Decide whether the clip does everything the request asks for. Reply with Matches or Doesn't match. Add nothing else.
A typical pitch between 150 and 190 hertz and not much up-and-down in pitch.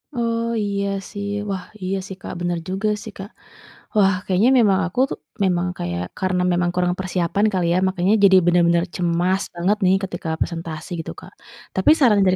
Matches